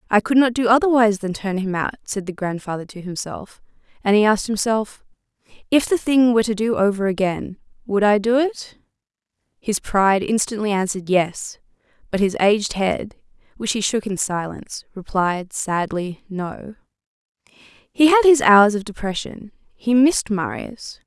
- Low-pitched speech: No, high, 210 Hz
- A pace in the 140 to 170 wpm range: Yes, average, 160 wpm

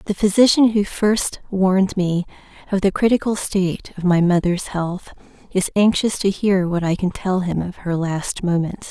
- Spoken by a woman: Yes, female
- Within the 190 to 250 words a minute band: No, average, 180 wpm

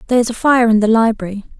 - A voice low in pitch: No, high, 225 Hz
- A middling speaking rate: No, fast, 265 wpm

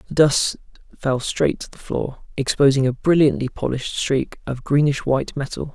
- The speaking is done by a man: Yes, male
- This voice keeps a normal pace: Yes, average, 165 wpm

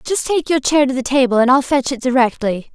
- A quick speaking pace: Yes, fast, 260 wpm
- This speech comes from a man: No, female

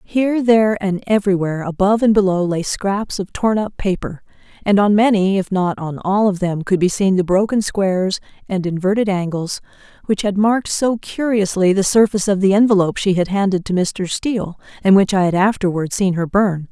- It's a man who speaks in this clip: No, female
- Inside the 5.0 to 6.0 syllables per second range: Yes, 5.5 syllables/s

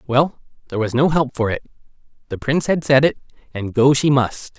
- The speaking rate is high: Yes, fast, 210 wpm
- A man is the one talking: Yes, male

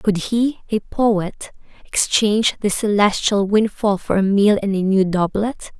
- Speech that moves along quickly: No, average, 155 wpm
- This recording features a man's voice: No, female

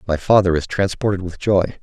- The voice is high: No, very low, 95 Hz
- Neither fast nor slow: Yes, average, 195 wpm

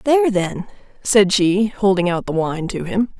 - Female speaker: Yes, female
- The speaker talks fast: No, average, 190 wpm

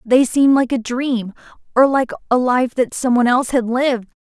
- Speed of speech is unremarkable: No, fast, 210 wpm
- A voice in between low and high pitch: No, very high, 250 Hz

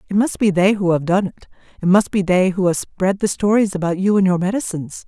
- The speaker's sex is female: Yes, female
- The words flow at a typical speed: No, fast, 250 wpm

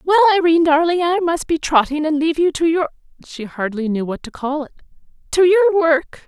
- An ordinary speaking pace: No, fast, 210 wpm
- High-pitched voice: Yes, very high, 320 Hz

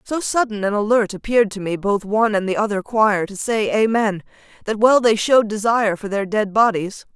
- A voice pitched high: Yes, high, 215 Hz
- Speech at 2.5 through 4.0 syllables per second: No, 5.5 syllables/s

